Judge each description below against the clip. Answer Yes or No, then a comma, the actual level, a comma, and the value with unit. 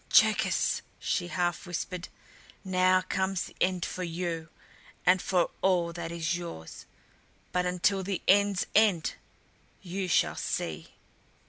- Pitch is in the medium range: Yes, medium, 180 Hz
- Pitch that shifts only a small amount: Yes, narrow, 1.6 semitones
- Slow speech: Yes, slow, 125 wpm